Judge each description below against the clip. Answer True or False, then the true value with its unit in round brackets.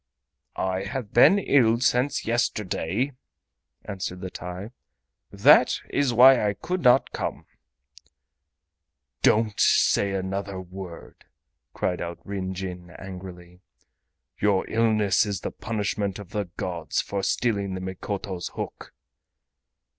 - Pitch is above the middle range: False (100 Hz)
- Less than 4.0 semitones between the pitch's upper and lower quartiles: True (3.5 semitones)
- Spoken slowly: True (115 wpm)